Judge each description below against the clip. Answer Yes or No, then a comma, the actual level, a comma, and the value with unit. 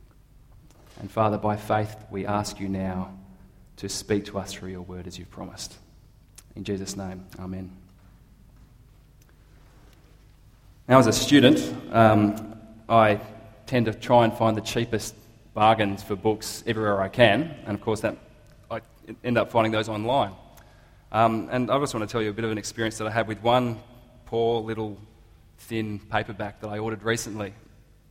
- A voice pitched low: Yes, low, 110 Hz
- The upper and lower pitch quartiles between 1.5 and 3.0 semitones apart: Yes, narrow, 2.4 semitones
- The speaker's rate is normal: Yes, average, 165 wpm